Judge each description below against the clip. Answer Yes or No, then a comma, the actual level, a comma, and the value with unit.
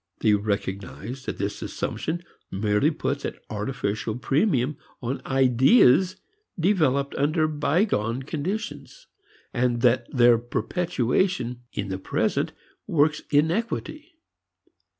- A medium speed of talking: No, slow, 100 wpm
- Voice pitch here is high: No, low, 135 Hz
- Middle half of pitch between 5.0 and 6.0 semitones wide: Yes, wide, 5.5 semitones